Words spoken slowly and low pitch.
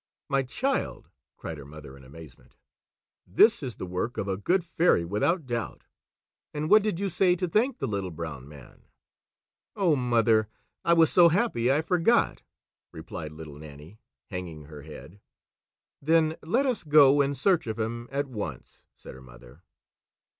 No: average, 160 wpm; low, 120 Hz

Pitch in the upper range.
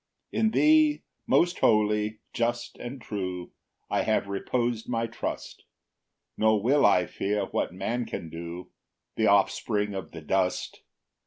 No: low, 105 Hz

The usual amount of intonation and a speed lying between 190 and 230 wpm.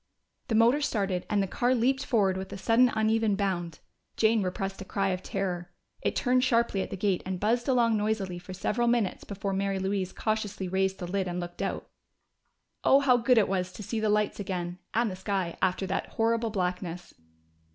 Yes: average, 3.4 semitones; average, 200 wpm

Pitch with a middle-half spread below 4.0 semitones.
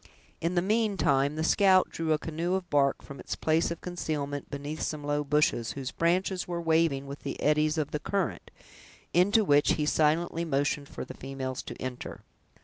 Yes: average, 3.3 semitones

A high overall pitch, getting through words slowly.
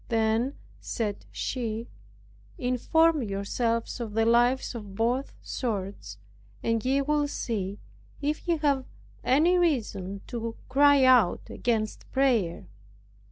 Yes: high, 235 Hz; slow, 115 wpm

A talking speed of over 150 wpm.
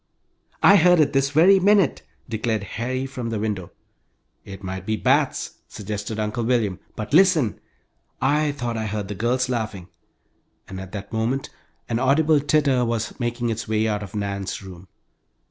Yes: average, 165 wpm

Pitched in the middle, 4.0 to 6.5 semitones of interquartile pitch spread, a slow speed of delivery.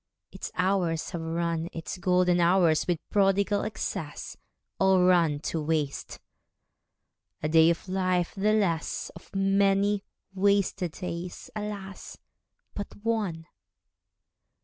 No: medium, 180 Hz; average, 2.8 semitones; slow, 110 wpm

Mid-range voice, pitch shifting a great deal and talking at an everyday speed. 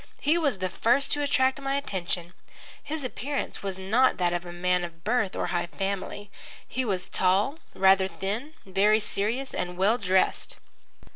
No: high, 200 Hz; wide, 5.9 semitones; average, 165 wpm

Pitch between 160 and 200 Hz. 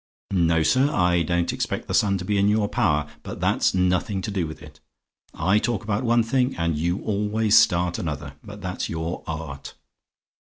No: very low, 90 Hz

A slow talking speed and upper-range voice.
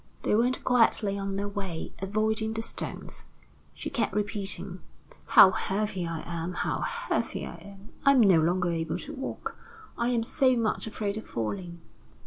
No: average, 165 wpm; high, 205 Hz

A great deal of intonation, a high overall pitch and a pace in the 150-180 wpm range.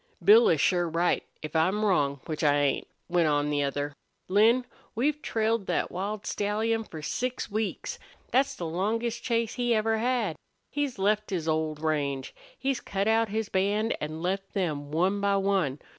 Yes: wide, 6.0 semitones; high, 195 Hz; average, 175 wpm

